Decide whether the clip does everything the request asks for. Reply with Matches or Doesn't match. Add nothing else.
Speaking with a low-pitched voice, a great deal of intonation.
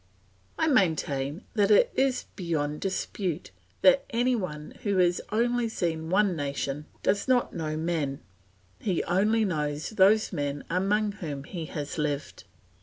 Doesn't match